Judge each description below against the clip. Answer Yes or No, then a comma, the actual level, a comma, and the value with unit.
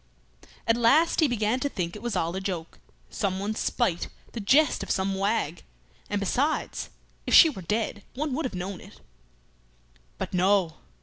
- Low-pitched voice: No, high, 205 Hz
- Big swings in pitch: No, average, 4.7 semitones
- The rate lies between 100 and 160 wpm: No, average, 170 wpm